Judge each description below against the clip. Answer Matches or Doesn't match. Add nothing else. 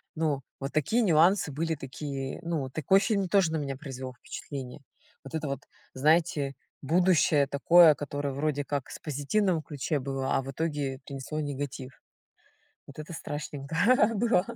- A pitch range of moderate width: Matches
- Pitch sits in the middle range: Matches